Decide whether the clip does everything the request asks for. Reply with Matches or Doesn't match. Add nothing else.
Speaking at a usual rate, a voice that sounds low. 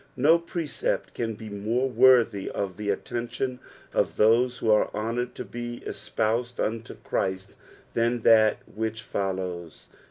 Doesn't match